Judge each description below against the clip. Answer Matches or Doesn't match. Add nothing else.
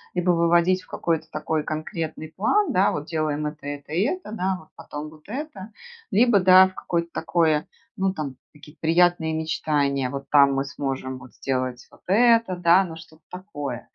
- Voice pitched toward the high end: Doesn't match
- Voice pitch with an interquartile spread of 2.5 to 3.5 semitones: Doesn't match